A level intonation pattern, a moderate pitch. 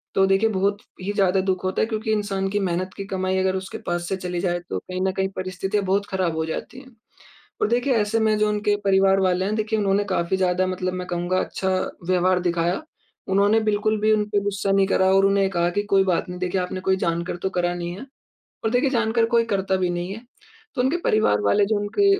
No: narrow, 2.3 semitones; high, 195 Hz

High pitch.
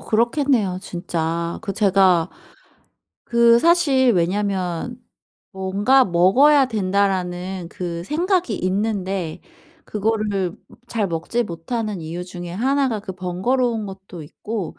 Yes: high, 195 Hz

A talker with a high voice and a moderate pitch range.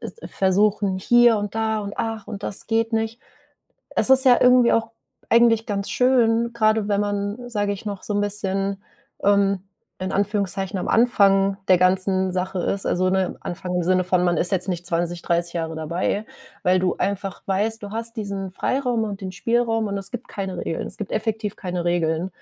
Yes: high, 200 Hz; average, 3.2 semitones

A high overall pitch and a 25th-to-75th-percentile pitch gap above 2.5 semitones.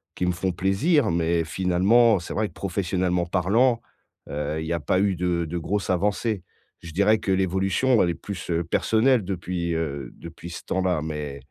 No: very low, 90 Hz; average, 2.9 semitones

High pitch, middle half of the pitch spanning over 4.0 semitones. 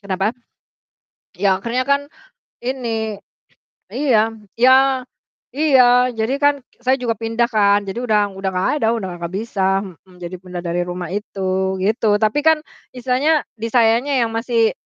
Yes: high, 225 Hz; average, 4.5 semitones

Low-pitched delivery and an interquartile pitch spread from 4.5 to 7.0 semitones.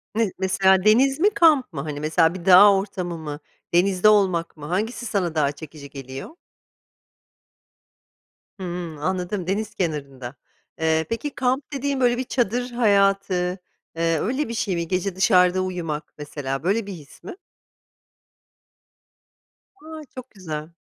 No: medium, 185 Hz; wide, 5.6 semitones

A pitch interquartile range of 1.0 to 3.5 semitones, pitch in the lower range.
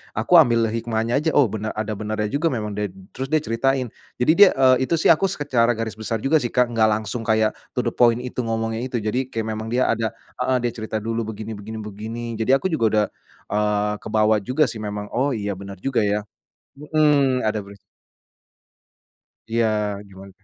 Yes: average, 3.1 semitones; low, 115 Hz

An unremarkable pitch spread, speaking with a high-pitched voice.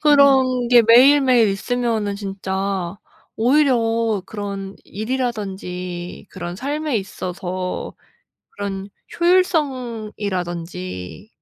Yes: average, 5.0 semitones; high, 215 Hz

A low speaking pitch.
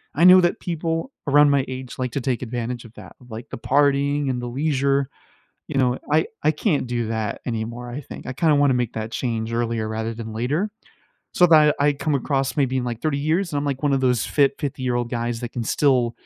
Yes: low, 130 Hz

